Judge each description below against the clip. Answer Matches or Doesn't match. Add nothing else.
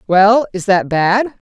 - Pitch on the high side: Matches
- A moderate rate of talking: Matches